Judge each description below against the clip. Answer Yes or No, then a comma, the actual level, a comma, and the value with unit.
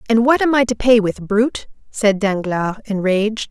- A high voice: Yes, high, 215 Hz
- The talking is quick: No, average, 190 wpm